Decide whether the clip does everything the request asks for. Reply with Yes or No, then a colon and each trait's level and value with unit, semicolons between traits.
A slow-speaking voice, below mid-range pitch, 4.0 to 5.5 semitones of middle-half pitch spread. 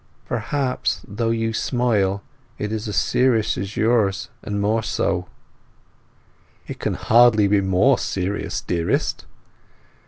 No: slow, 120 wpm; low, 105 Hz; average, 2.7 semitones